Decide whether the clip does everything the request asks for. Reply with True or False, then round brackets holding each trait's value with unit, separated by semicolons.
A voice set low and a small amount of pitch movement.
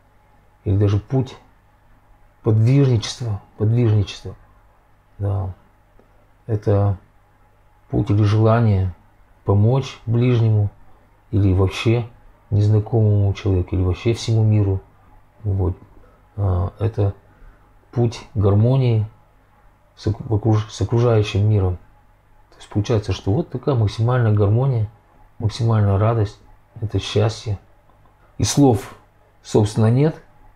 True (105 Hz; 2.3 semitones)